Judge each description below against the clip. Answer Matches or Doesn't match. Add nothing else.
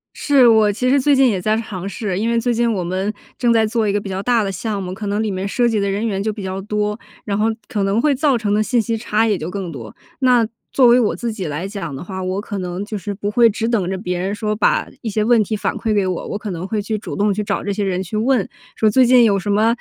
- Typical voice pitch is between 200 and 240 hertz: Matches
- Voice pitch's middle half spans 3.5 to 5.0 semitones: Doesn't match